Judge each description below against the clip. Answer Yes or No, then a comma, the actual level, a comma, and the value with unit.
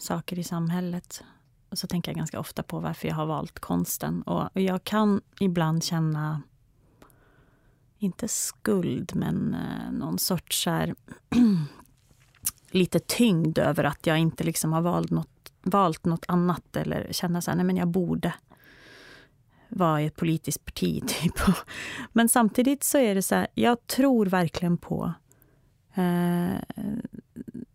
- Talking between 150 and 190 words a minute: No, average, 140 wpm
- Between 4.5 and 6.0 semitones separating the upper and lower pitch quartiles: Yes, wide, 5.6 semitones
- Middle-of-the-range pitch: Yes, medium, 175 Hz